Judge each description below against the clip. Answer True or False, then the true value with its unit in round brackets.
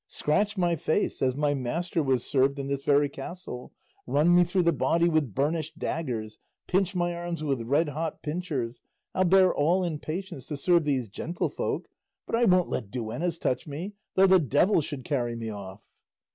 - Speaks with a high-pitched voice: False (155 Hz)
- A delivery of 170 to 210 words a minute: True (185 wpm)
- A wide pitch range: False (4.6 semitones)